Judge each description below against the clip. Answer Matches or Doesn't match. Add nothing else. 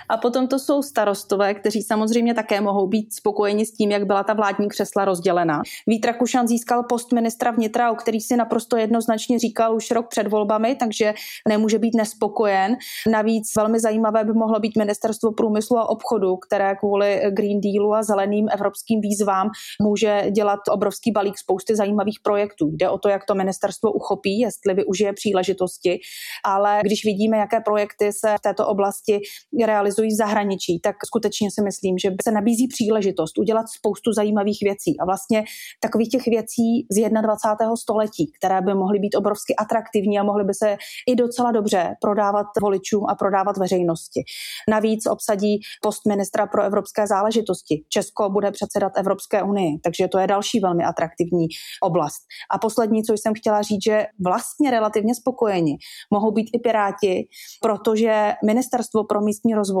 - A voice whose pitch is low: Doesn't match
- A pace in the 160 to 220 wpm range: Matches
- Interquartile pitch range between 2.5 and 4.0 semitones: Doesn't match